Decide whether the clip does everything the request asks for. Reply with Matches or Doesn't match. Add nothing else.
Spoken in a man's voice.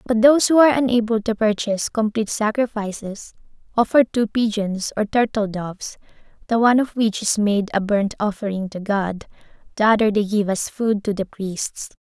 Doesn't match